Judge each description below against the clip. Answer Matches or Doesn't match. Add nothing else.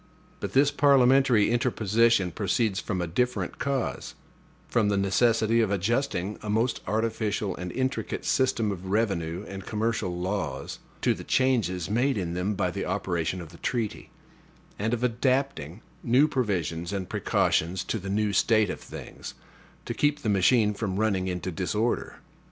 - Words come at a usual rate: Matches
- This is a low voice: Matches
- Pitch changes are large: Doesn't match